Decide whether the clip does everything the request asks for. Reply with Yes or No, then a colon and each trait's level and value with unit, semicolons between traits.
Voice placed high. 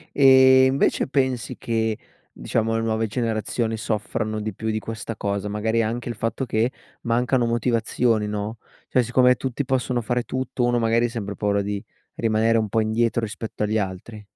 No: low, 115 Hz